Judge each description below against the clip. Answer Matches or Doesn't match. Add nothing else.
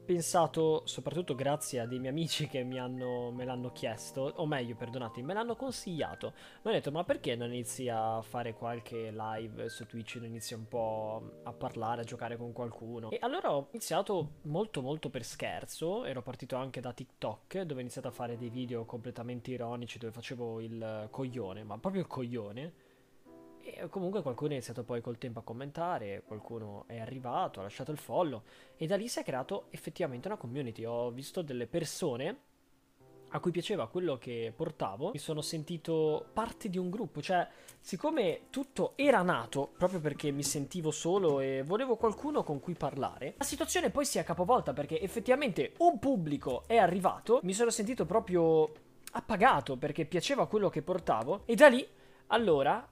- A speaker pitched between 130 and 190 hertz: Matches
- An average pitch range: Doesn't match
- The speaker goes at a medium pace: Doesn't match